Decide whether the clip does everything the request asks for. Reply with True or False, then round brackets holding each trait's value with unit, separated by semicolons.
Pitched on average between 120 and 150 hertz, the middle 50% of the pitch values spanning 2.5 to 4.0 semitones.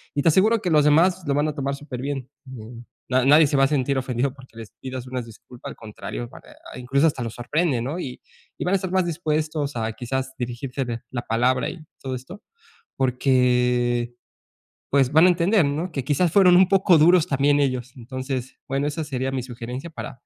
True (135 Hz; 3.7 semitones)